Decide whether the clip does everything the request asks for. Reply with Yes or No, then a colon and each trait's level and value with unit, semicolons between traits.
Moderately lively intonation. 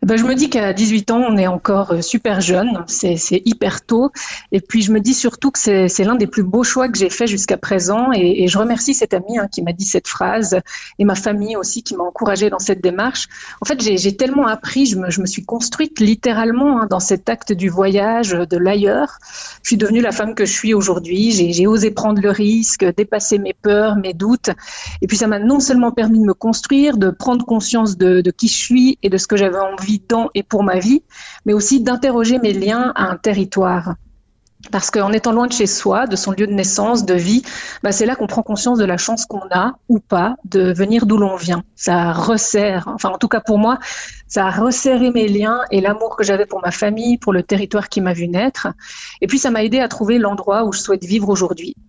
Yes: average, 3.2 semitones